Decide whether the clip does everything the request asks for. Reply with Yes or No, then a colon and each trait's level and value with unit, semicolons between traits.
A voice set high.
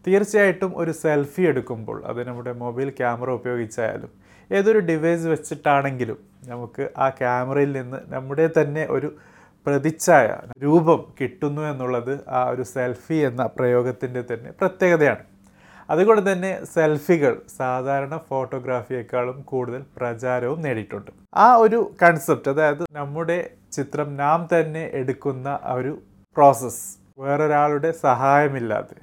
No: medium, 140 Hz